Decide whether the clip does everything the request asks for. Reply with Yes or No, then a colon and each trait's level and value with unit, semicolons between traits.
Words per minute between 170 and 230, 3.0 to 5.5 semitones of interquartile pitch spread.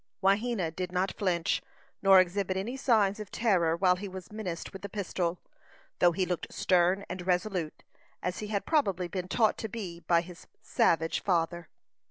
No: average, 175 wpm; narrow, 2.5 semitones